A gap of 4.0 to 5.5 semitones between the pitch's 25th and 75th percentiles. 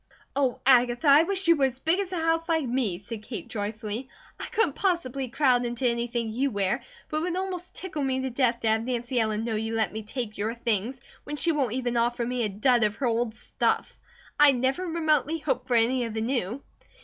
Yes: average, 4.4 semitones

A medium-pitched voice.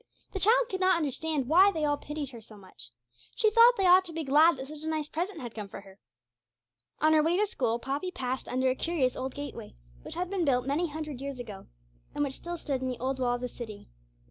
No: very high, 290 Hz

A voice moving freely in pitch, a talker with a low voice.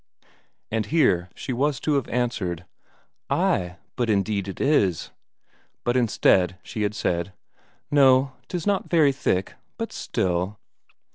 Yes: wide, 6.6 semitones; low, 110 Hz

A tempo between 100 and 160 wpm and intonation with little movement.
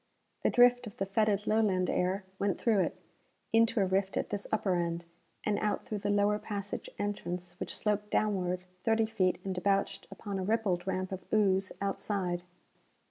No: average, 175 wpm; narrow, 2.3 semitones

